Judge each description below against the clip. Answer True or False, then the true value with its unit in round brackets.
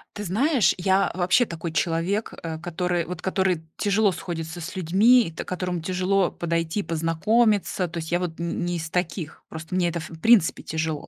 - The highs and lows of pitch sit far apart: False (2.7 semitones)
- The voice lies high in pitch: False (175 Hz)